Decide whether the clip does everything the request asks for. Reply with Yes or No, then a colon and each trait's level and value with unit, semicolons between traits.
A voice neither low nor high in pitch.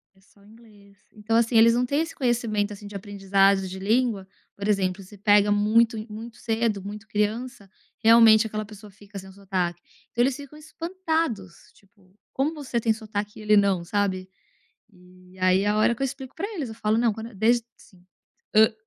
No: high, 210 Hz